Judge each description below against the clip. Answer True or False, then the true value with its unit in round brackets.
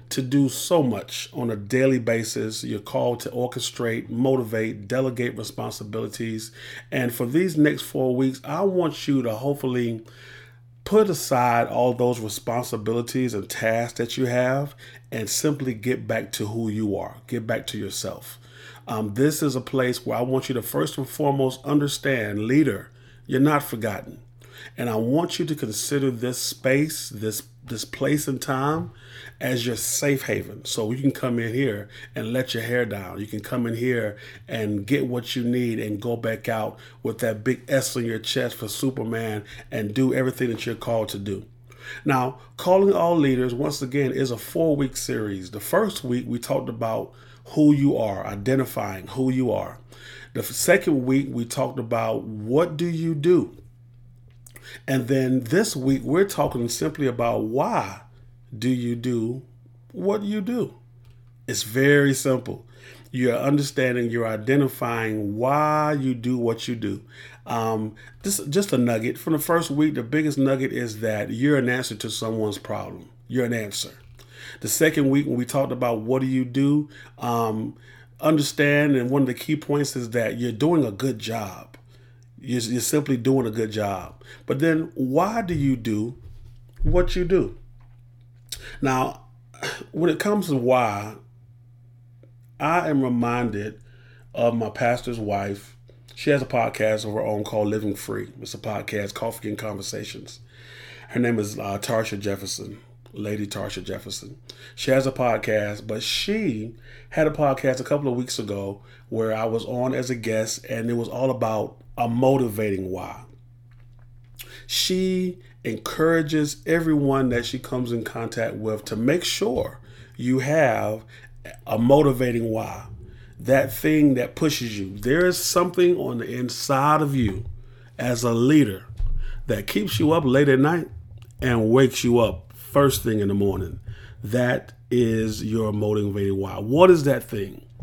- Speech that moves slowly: False (165 wpm)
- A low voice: True (120 Hz)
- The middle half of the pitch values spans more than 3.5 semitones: False (2.9 semitones)